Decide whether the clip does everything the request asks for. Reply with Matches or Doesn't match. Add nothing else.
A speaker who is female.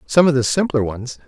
Doesn't match